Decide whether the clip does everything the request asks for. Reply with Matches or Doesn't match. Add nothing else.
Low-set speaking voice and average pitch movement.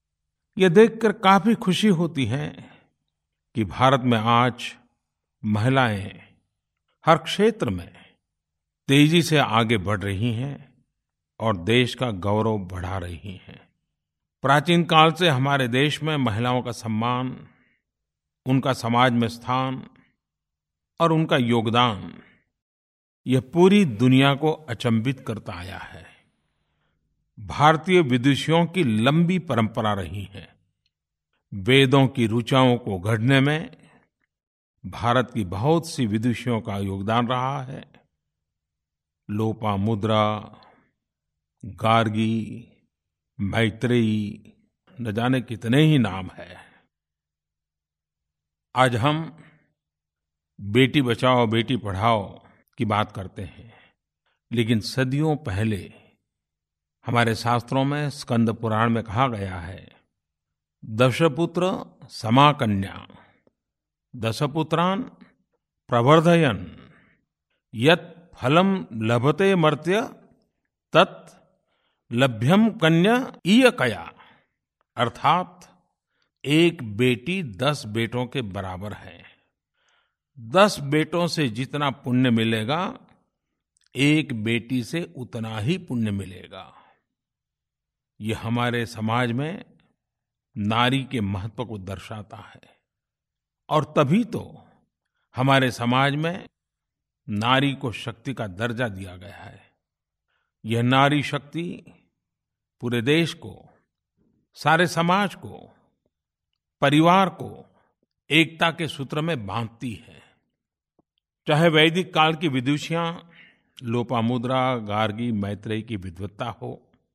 Doesn't match